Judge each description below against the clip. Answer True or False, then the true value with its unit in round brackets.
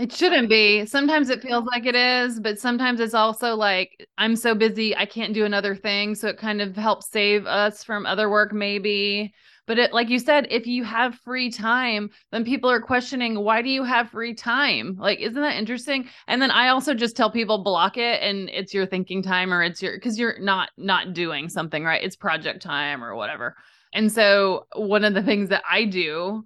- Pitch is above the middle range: True (215 Hz)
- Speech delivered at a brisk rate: True (215 wpm)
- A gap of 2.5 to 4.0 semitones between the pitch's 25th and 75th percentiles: True (3.1 semitones)